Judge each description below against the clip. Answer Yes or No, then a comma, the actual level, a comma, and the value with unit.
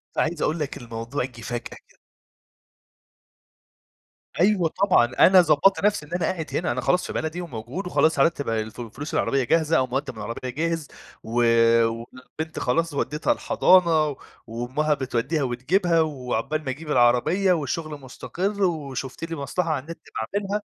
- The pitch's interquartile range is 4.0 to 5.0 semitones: Yes, average, 4.7 semitones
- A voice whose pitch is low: No, medium, 150 Hz